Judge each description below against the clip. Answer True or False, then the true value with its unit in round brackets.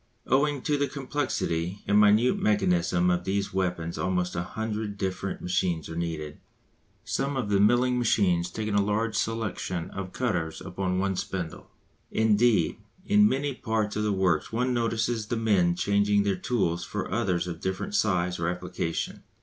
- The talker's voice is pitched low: True (100 Hz)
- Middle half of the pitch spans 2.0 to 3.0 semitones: False (4.1 semitones)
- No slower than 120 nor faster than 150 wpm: False (160 wpm)